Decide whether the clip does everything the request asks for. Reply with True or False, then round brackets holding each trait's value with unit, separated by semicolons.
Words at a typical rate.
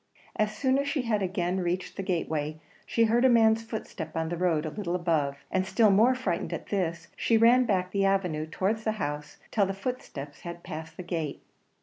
False (210 wpm)